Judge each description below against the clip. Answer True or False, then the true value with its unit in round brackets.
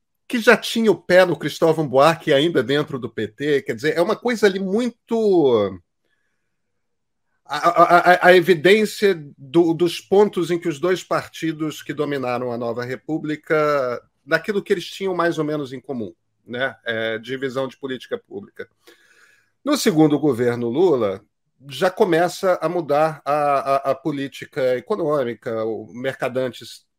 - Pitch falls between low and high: True (155 Hz)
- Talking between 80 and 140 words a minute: False (150 wpm)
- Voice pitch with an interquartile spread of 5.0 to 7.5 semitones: True (5.3 semitones)